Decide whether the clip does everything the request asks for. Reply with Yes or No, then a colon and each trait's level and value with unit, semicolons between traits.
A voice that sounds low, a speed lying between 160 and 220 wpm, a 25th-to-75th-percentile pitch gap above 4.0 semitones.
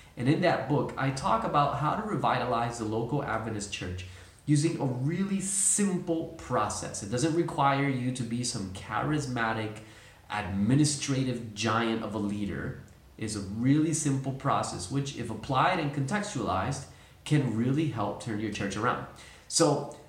No: low, 125 Hz; average, 150 wpm; average, 5.3 semitones